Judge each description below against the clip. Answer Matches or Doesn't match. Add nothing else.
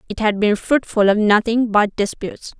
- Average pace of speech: Matches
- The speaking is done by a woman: Matches